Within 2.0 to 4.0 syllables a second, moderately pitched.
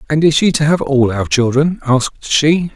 No: 4.9 syllables/s; medium, 145 Hz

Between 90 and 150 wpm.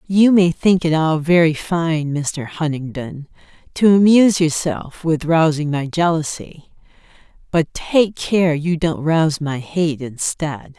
Yes: average, 140 wpm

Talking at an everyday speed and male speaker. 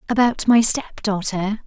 No: average, 145 wpm; female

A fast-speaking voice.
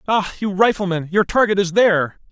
No: average, 180 wpm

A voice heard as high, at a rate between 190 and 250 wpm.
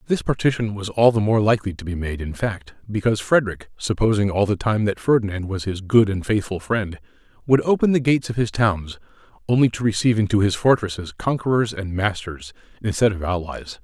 No: low, 105 Hz; average, 195 wpm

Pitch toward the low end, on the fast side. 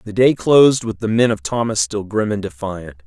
Yes: low, 105 Hz; fast, 235 wpm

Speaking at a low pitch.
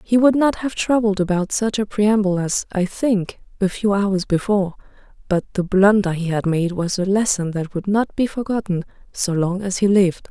No: high, 195 Hz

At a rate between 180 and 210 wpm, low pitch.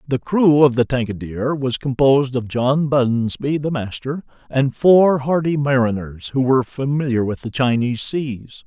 No: average, 160 wpm; low, 130 Hz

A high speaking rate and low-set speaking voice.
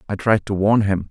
Yes: fast, 270 wpm; low, 100 Hz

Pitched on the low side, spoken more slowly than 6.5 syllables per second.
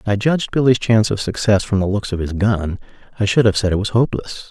No: low, 105 Hz; 6.6 syllables/s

